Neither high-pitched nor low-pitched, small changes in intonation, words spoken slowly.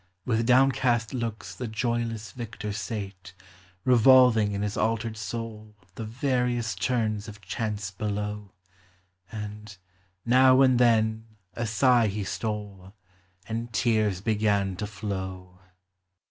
No: low, 110 Hz; narrow, 2.3 semitones; slow, 115 wpm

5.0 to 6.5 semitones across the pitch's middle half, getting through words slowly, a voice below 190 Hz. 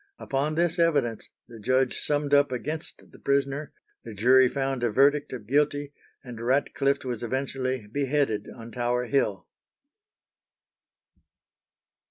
No: average, 2.9 semitones; slow, 125 wpm; low, 135 Hz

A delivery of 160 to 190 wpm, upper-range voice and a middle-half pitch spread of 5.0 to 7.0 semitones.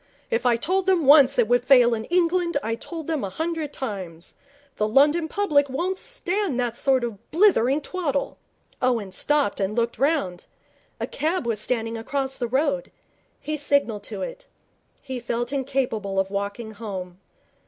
Yes: average, 165 wpm; very high, 265 Hz; wide, 5.6 semitones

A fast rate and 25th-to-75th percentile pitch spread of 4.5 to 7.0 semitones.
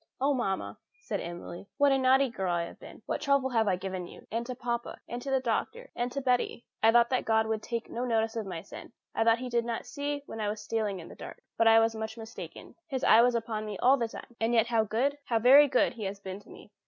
No: fast, 275 wpm; average, 2.8 semitones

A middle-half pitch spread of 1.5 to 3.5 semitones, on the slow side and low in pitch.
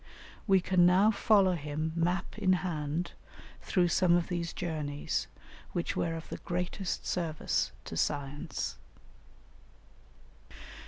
No: average, 2.7 semitones; slow, 115 wpm; medium, 175 Hz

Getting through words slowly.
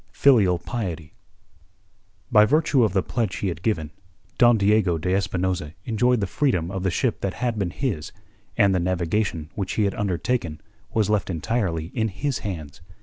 No: average, 170 wpm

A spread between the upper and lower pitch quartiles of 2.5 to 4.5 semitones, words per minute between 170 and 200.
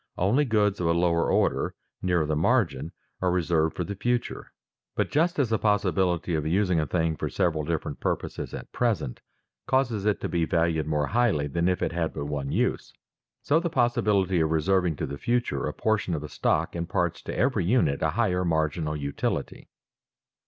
No: average, 5.0 semitones; average, 190 wpm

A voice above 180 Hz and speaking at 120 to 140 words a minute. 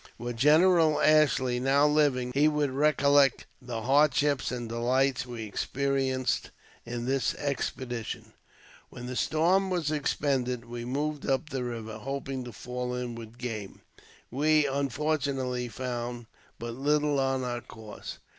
No: low, 130 Hz; slow, 135 wpm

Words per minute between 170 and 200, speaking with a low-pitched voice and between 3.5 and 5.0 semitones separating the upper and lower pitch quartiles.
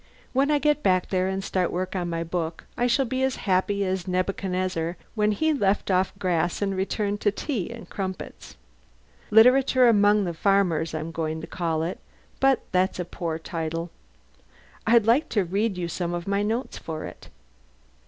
No: average, 180 wpm; high, 190 Hz; average, 3.8 semitones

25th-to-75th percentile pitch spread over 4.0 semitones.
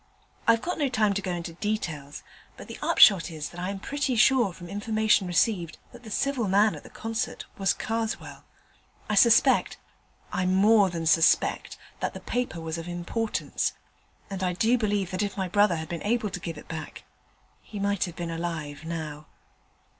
Yes: average, 4.5 semitones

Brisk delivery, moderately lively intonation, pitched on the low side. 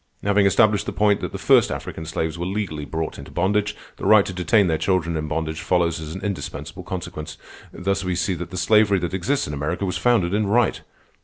Yes: fast, 220 wpm; average, 3.9 semitones; very low, 90 Hz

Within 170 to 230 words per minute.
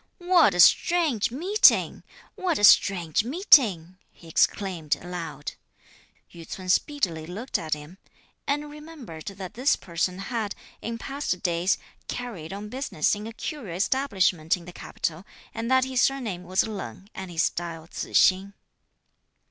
No: average, 145 wpm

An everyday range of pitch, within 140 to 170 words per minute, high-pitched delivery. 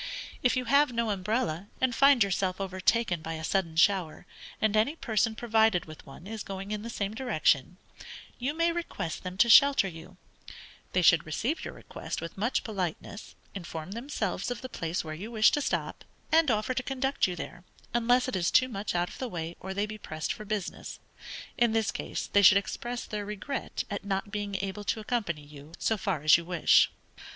No: average, 5.0 semitones; average, 200 wpm; high, 205 Hz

